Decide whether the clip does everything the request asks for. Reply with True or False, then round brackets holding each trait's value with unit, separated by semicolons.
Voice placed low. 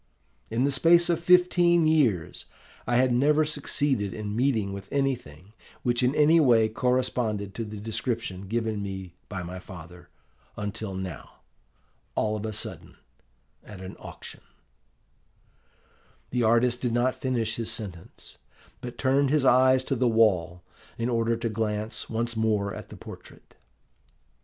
True (115 Hz)